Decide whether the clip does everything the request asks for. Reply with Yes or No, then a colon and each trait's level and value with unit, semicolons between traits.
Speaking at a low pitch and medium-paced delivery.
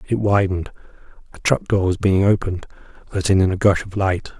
Yes: very low, 95 Hz; average, 190 wpm